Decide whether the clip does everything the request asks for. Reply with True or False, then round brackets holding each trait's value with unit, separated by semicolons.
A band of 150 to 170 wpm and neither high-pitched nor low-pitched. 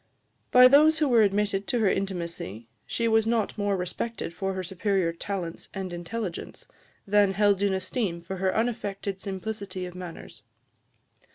False (155 wpm; 195 Hz)